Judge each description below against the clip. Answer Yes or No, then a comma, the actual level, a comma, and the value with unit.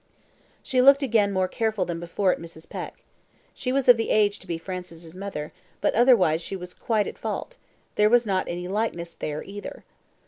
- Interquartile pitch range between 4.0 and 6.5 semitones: Yes, average, 4.6 semitones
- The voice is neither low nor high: No, high, 195 Hz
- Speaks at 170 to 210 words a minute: Yes, average, 195 wpm